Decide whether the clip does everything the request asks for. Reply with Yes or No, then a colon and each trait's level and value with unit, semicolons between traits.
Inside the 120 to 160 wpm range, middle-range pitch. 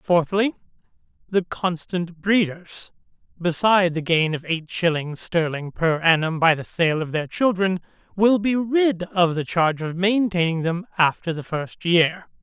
Yes: average, 155 wpm; medium, 175 Hz